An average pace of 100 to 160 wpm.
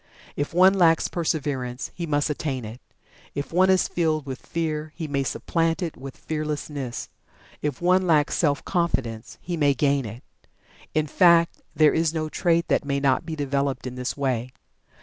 No: average, 170 wpm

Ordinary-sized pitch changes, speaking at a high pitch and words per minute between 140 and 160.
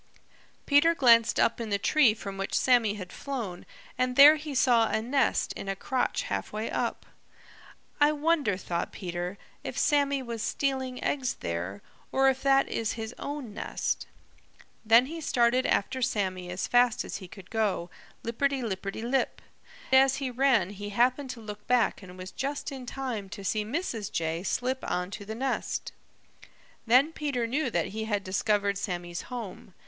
No: average, 5.0 semitones; high, 230 Hz; average, 170 wpm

